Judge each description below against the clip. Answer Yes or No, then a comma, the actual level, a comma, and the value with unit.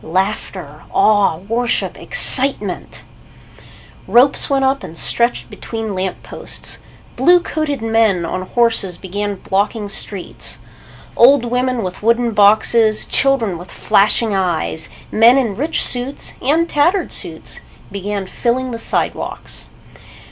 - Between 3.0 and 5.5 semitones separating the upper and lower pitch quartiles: Yes, average, 4.4 semitones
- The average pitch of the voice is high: Yes, high, 225 Hz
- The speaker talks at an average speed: No, slow, 120 wpm